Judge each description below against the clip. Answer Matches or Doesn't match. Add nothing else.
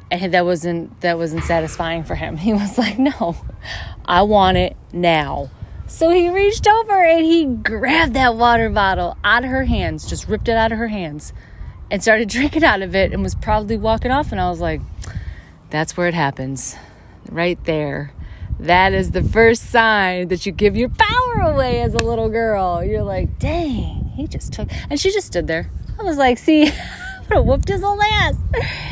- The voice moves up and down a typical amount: Doesn't match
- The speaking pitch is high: Matches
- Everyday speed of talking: Matches